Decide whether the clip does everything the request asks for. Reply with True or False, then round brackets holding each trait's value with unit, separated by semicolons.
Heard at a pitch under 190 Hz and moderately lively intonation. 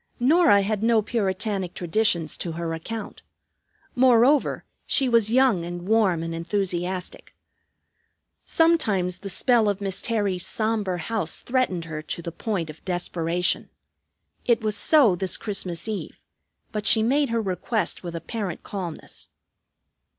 False (200 Hz; 4.5 semitones)